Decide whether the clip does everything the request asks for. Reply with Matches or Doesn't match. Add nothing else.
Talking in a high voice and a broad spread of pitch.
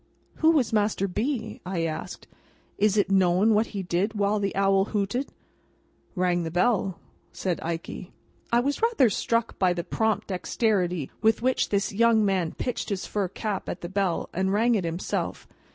Doesn't match